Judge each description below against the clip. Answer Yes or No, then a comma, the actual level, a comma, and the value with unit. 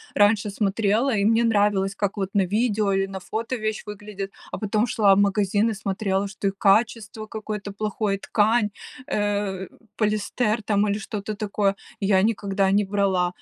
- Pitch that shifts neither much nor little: No, narrow, 1.5 semitones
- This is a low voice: No, high, 205 Hz